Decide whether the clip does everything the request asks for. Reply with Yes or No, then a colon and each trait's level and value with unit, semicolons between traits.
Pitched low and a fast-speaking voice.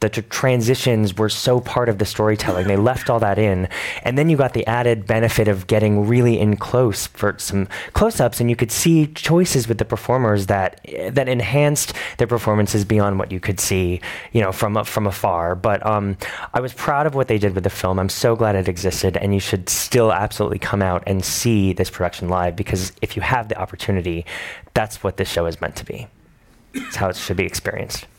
Yes: low, 105 Hz; fast, 215 wpm